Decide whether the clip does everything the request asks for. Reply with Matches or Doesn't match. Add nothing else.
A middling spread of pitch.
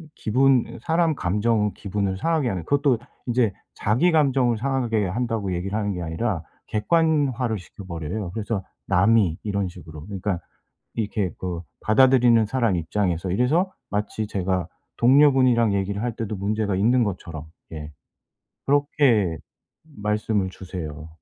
Matches